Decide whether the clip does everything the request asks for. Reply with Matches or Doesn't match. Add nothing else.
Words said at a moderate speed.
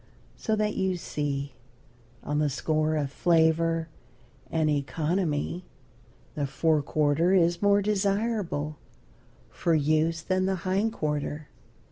Doesn't match